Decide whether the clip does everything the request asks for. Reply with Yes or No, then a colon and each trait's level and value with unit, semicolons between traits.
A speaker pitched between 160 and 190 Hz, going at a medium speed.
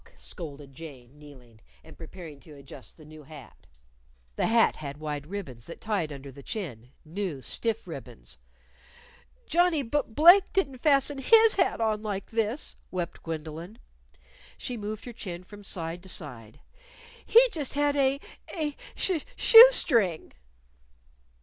Yes: medium, 185 Hz; average, 145 wpm